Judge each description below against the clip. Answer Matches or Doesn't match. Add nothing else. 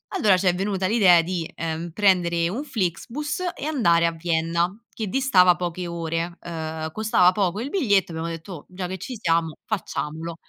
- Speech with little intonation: Doesn't match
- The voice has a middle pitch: Matches